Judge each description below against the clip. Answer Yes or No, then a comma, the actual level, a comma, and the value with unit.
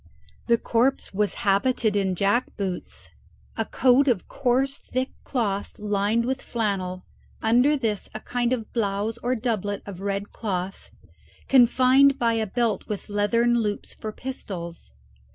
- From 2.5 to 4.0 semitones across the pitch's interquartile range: Yes, average, 3.6 semitones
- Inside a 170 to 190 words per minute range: No, slow, 135 wpm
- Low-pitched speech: No, high, 225 Hz